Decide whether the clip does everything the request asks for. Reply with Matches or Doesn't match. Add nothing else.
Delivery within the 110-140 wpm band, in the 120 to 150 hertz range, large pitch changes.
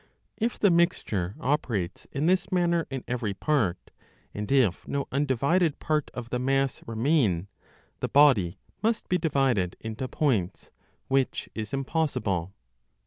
Matches